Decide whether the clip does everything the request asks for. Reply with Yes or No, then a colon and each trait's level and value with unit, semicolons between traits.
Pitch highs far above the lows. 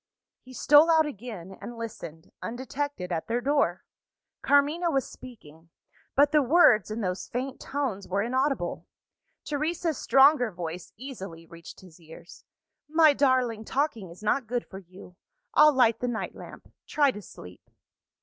Yes: wide, 7.3 semitones